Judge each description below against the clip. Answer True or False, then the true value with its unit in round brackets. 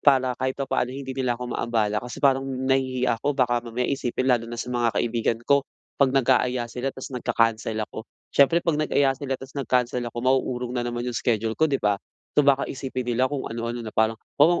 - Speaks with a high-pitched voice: False (125 Hz)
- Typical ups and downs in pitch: False (2.1 semitones)